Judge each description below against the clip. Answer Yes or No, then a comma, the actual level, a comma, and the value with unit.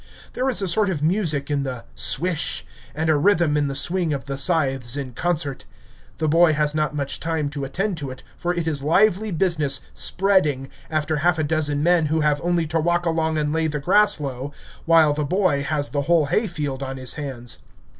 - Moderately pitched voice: Yes, medium, 155 Hz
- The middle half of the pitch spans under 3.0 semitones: No, average, 3.4 semitones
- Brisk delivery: Yes, fast, 210 wpm